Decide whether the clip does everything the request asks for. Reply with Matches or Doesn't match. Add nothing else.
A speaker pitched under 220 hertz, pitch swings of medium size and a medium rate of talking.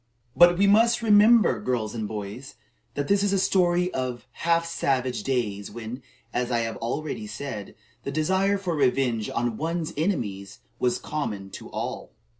Doesn't match